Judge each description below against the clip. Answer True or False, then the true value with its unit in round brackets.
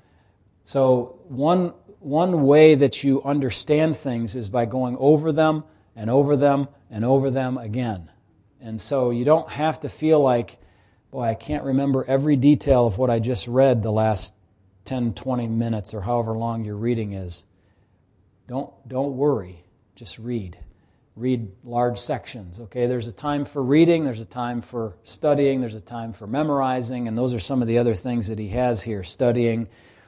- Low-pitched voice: True (120 Hz)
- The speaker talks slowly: False (175 wpm)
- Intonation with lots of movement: False (3.8 semitones)